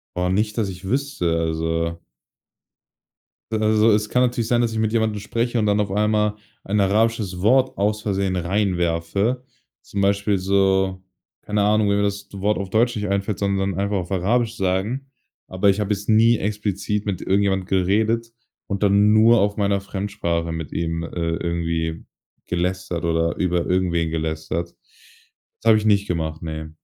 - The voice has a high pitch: No, low, 100 Hz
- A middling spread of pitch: Yes, average, 3.1 semitones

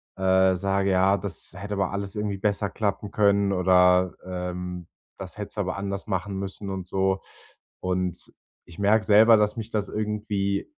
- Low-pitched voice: Yes, low, 100 Hz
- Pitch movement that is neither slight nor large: No, narrow, 1.7 semitones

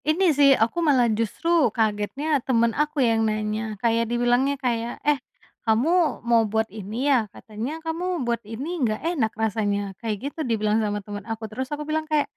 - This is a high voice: Yes, high, 235 Hz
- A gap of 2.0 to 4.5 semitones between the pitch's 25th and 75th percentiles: No, average, 5.0 semitones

